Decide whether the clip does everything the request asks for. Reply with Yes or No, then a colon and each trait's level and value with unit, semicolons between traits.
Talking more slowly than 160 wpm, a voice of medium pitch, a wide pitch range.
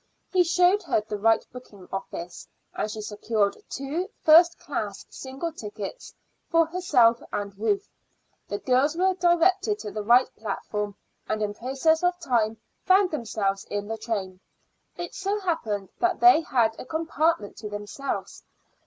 No: average, 150 wpm; very high, 255 Hz; wide, 8.5 semitones